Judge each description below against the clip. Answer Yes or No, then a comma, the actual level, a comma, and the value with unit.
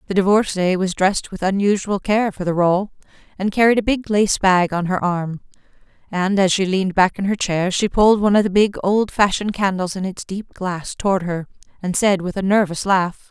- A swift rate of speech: Yes, fast, 215 wpm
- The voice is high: Yes, high, 195 Hz